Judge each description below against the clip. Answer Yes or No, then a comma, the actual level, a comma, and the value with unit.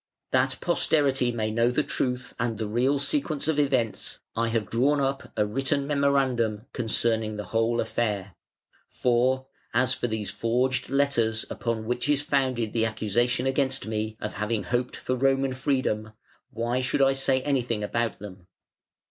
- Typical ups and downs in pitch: Yes, average, 3.3 semitones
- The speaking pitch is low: Yes, low, 120 Hz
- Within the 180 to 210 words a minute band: No, average, 155 wpm